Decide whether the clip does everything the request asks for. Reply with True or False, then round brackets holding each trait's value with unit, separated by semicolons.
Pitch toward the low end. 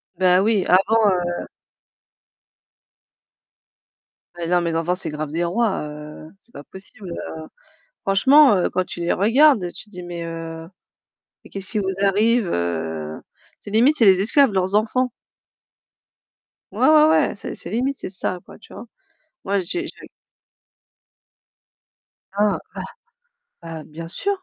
False (190 Hz)